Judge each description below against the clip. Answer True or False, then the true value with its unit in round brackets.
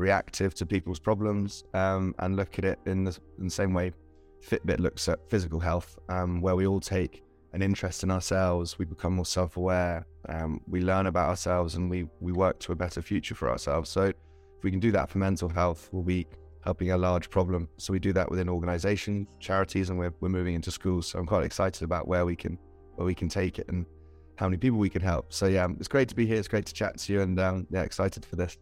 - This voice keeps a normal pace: False (240 wpm)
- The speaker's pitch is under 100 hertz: True (90 Hz)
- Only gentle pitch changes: True (2.0 semitones)